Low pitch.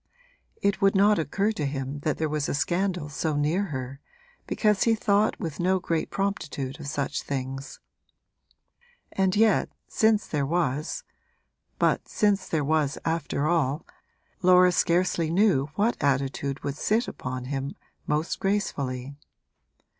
No: medium, 160 Hz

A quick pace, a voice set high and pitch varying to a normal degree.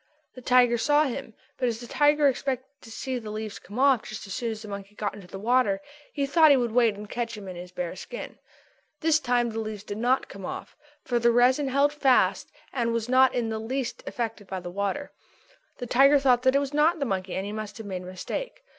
Yes: fast, 250 wpm; high, 240 Hz; average, 4.2 semitones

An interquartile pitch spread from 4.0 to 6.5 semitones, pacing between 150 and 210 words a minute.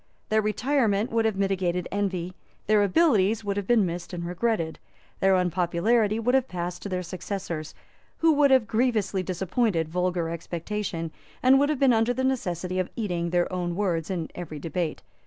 Yes: average, 4.3 semitones; average, 175 wpm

